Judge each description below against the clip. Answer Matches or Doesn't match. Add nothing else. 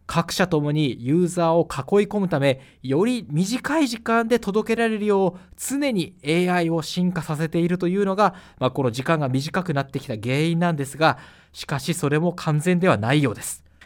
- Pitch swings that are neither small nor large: Matches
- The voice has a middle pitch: Matches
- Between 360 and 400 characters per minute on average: Matches